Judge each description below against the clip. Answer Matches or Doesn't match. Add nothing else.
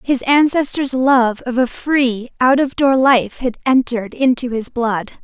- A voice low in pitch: Doesn't match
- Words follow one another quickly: Doesn't match